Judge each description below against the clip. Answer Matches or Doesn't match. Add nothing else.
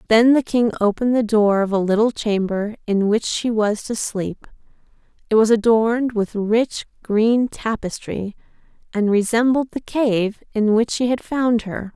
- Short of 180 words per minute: Matches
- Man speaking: Doesn't match